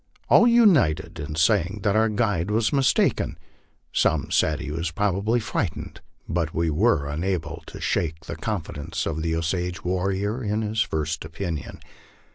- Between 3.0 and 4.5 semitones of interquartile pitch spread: No, average, 4.9 semitones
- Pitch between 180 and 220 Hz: No, very low, 90 Hz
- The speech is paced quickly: No, average, 155 wpm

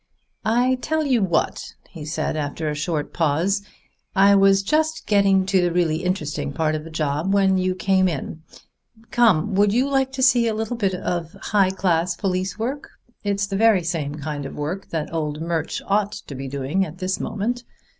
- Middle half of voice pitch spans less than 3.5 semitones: No, average, 4.4 semitones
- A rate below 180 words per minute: No, average, 190 wpm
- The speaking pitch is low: No, medium, 185 Hz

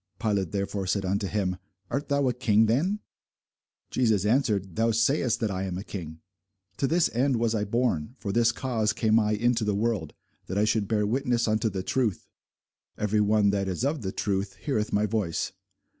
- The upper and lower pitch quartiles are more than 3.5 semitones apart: No, average, 3.2 semitones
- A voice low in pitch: Yes, low, 110 Hz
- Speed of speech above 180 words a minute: Yes, average, 195 wpm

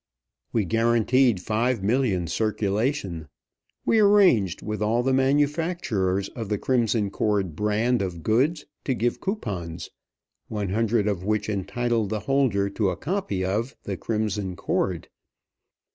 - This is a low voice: Yes, low, 110 Hz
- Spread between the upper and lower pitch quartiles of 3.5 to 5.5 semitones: Yes, average, 4.2 semitones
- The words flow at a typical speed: No, slow, 130 wpm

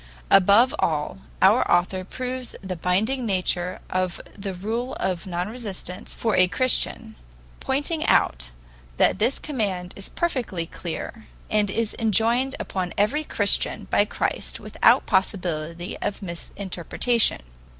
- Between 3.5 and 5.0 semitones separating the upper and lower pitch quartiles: Yes, average, 4.7 semitones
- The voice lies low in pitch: No, high, 195 Hz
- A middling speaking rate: No, slow, 125 wpm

